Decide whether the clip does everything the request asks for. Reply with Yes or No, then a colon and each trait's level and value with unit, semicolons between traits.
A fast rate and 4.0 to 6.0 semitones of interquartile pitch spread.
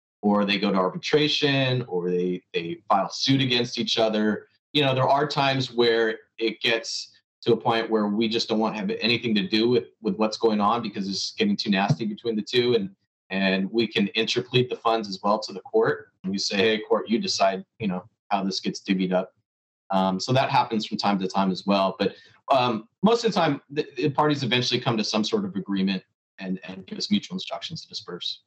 Yes: fast, 225 wpm; average, 4.7 semitones